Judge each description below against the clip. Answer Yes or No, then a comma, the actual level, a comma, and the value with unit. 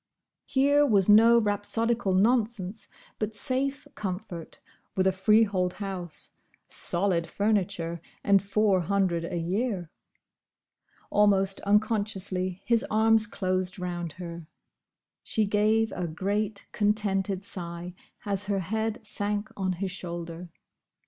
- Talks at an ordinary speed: No, slow, 110 wpm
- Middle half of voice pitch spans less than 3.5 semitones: Yes, average, 2.9 semitones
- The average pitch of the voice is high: Yes, high, 200 Hz